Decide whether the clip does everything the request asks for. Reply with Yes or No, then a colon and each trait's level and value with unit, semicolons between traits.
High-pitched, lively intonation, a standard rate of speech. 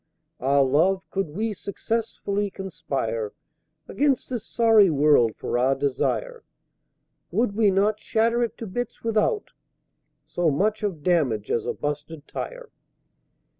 No: high, 195 Hz; wide, 7.4 semitones; slow, 130 wpm